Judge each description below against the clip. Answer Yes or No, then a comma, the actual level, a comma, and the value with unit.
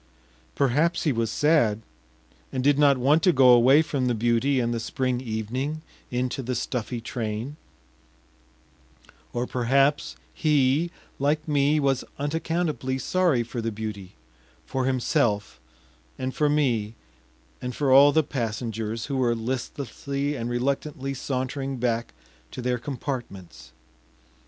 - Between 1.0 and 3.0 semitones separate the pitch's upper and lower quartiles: No, average, 3.4 semitones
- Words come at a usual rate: No, slow, 130 wpm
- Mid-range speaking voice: No, low, 130 Hz